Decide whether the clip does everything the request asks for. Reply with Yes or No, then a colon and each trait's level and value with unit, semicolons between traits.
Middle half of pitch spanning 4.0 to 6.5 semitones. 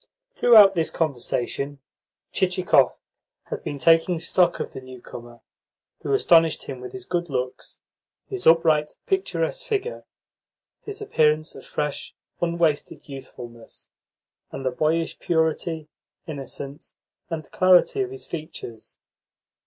Yes: average, 4.9 semitones